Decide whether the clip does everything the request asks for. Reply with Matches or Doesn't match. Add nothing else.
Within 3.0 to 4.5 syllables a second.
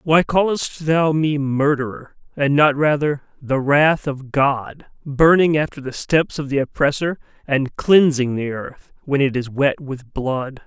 Matches